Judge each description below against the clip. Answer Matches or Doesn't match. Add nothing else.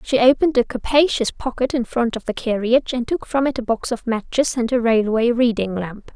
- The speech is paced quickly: Matches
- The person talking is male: Doesn't match